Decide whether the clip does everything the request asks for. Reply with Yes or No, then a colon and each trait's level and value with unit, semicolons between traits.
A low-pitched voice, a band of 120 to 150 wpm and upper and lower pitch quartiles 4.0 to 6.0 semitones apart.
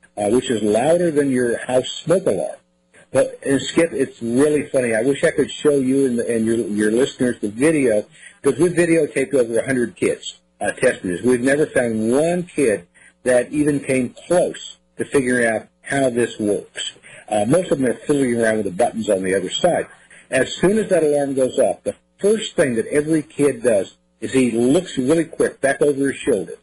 No: low, 130 Hz; fast, 205 wpm; average, 4.3 semitones